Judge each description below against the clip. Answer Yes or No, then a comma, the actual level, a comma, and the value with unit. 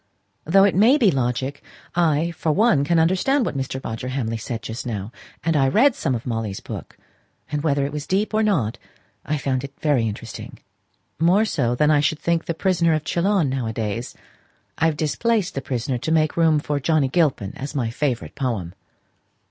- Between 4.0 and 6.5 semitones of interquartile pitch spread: Yes, average, 5.2 semitones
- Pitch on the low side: No, medium, 145 Hz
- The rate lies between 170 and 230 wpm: Yes, average, 195 wpm